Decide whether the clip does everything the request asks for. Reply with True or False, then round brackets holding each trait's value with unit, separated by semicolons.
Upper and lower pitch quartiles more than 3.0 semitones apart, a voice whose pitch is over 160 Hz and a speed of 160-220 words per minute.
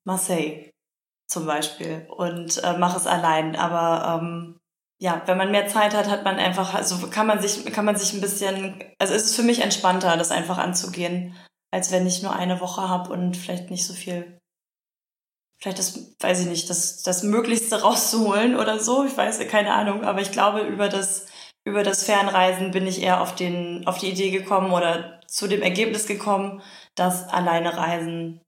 False (2.5 semitones; 185 Hz; 190 wpm)